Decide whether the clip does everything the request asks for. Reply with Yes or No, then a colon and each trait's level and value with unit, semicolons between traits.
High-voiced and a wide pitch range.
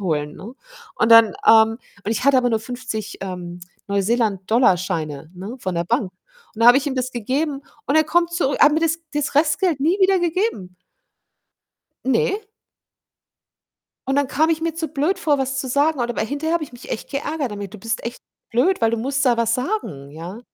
Yes: very high, 250 Hz; wide, 5.8 semitones